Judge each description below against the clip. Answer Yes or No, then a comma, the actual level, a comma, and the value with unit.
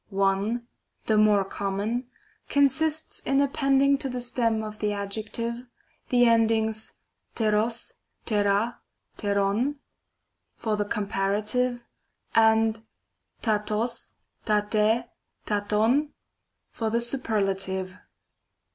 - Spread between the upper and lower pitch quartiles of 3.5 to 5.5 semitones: No, average, 2.7 semitones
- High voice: Yes, high, 220 Hz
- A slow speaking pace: Yes, slow, 90 wpm